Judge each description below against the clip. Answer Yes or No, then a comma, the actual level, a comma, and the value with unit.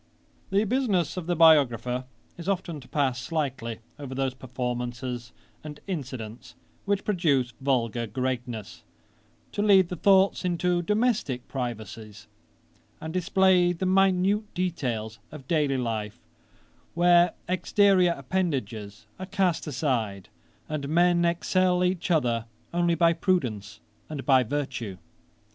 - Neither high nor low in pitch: Yes, medium, 150 Hz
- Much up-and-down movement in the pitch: Yes, wide, 6.6 semitones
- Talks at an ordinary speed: No, slow, 120 wpm